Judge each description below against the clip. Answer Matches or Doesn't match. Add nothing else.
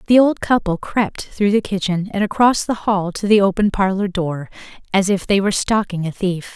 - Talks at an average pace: Doesn't match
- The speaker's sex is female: Matches